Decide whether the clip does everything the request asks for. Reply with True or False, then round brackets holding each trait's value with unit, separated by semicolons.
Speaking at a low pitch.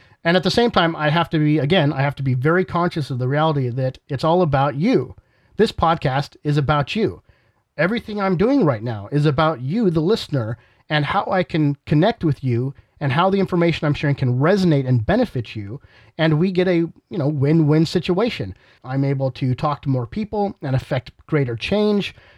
False (150 Hz)